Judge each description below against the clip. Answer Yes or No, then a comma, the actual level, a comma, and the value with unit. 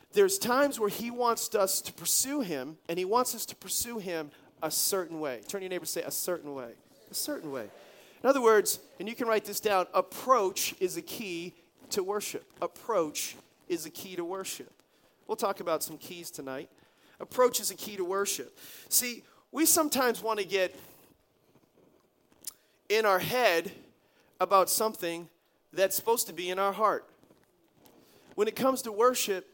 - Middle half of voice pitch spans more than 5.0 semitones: Yes, wide, 5.4 semitones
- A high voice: Yes, high, 200 Hz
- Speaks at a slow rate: No, average, 175 wpm